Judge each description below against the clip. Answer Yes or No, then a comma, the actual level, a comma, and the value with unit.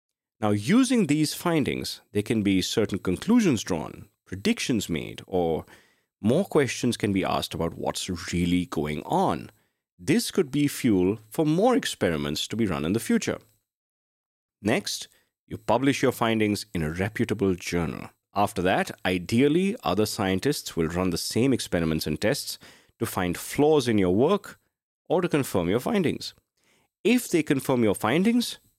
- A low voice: Yes, low, 110 Hz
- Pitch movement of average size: No, wide, 8.4 semitones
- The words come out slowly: No, average, 150 wpm